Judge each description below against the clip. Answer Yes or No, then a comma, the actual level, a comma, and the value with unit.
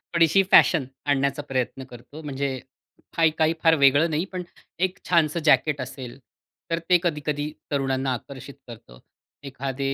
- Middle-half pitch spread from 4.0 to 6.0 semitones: No, average, 3.3 semitones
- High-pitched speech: No, medium, 140 Hz